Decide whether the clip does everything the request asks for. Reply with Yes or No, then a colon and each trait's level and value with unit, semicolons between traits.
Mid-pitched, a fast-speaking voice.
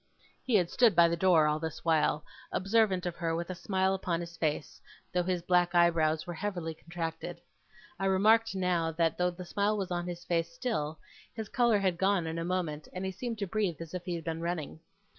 Yes: medium, 175 Hz; fast, 215 wpm